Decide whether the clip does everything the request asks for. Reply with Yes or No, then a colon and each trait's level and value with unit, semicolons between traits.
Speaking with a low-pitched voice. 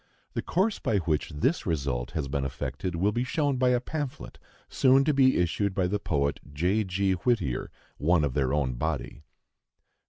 Yes: very low, 90 Hz